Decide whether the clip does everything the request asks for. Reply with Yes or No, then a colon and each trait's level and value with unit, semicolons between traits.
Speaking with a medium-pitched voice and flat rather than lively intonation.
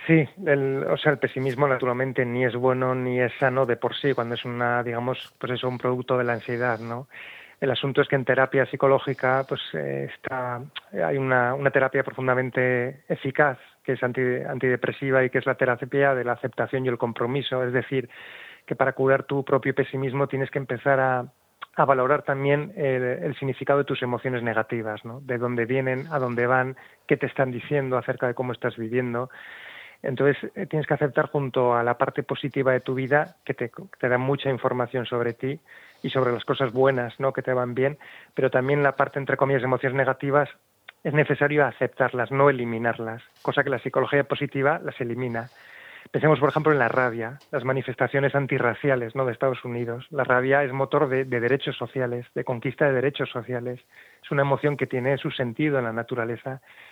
No: low, 130 Hz; narrow, 1.8 semitones